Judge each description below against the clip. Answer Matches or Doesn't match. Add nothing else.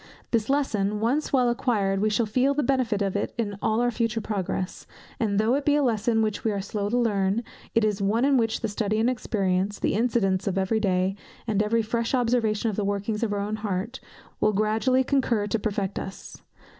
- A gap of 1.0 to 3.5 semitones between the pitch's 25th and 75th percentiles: Matches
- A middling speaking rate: Doesn't match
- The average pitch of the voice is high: Matches